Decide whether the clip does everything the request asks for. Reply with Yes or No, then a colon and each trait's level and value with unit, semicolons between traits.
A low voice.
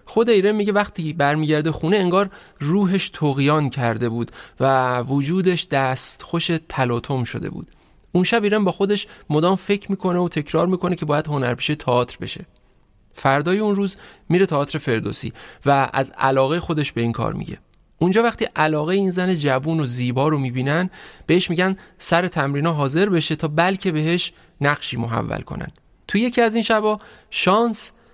No: medium, 165 Hz